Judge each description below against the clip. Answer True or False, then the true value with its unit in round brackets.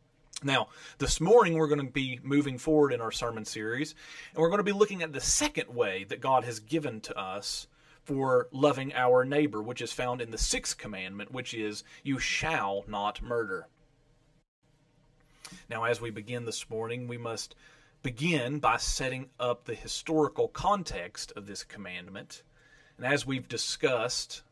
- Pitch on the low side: False (145 Hz)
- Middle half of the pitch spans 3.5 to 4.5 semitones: True (4.2 semitones)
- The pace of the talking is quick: False (165 wpm)